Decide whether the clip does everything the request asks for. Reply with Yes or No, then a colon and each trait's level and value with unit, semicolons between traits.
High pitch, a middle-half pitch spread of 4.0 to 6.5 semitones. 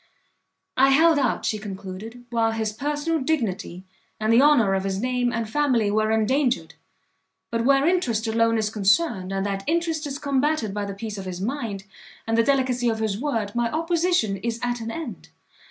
Yes: high, 230 Hz; average, 4.9 semitones